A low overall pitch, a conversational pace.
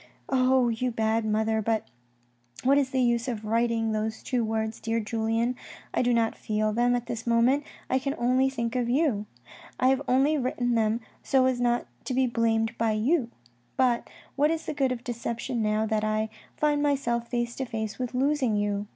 No: high, 235 Hz; average, 195 wpm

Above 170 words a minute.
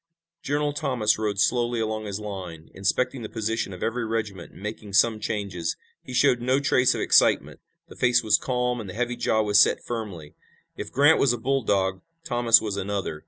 Yes: average, 190 wpm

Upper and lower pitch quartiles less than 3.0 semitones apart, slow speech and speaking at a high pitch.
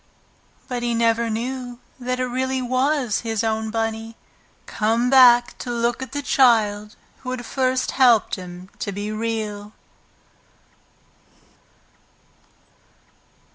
Yes: narrow, 2.4 semitones; slow, 115 wpm; high, 235 Hz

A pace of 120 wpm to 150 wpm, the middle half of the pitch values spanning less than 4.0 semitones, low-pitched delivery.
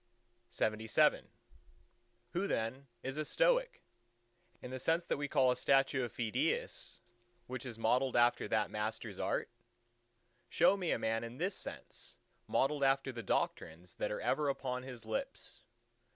Yes: average, 145 wpm; average, 3.5 semitones; low, 125 Hz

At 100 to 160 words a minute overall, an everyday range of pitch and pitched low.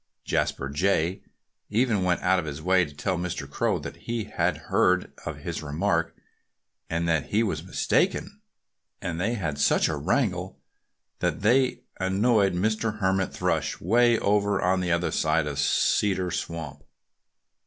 Yes: average, 155 wpm; average, 3.8 semitones; very low, 90 Hz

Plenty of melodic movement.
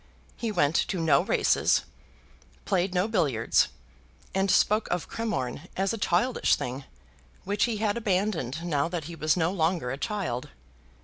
No: average, 4.8 semitones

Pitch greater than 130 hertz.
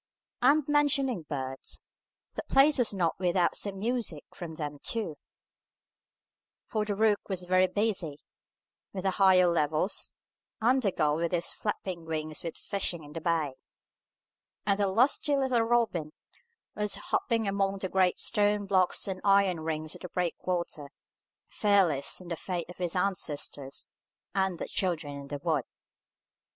Yes: medium, 185 Hz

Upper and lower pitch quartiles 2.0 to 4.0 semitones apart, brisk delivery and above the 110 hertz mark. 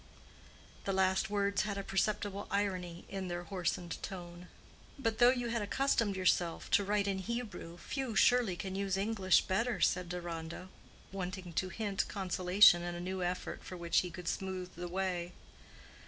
No: narrow, 2.4 semitones; average, 165 wpm; high, 190 Hz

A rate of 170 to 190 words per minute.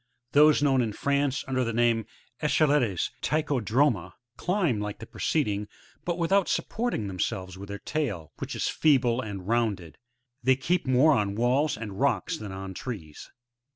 No: average, 160 wpm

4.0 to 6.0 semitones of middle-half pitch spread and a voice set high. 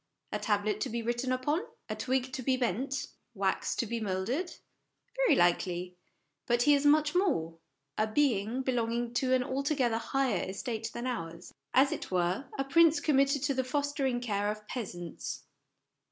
Yes: average, 4.6 semitones; high, 245 Hz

